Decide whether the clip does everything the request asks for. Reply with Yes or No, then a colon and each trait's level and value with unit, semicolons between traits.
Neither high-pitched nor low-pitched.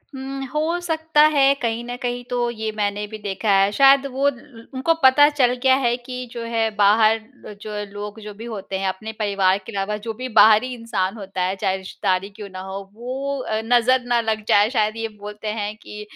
No: high, 220 Hz